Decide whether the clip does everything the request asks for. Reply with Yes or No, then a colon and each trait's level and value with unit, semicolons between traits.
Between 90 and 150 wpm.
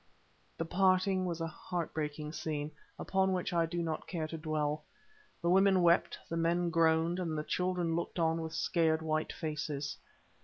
No: average, 170 wpm